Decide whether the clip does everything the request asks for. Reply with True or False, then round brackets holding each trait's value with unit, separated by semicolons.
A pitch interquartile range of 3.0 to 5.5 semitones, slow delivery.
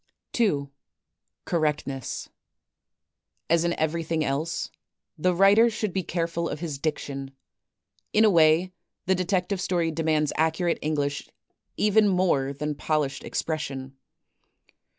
True (3.5 semitones; 110 wpm)